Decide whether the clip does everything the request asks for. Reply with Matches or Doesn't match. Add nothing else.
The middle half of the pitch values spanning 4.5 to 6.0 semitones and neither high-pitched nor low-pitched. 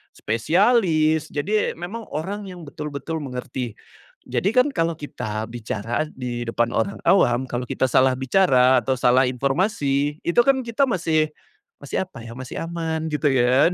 Matches